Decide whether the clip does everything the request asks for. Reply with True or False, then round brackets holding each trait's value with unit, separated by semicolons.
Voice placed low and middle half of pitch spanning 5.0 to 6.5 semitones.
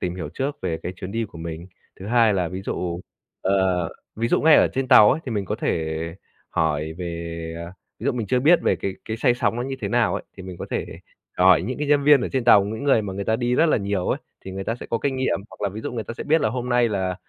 True (105 Hz; 5.3 semitones)